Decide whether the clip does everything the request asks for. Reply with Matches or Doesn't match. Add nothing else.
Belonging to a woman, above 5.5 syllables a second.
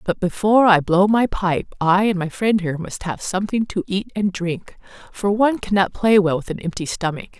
Doesn't match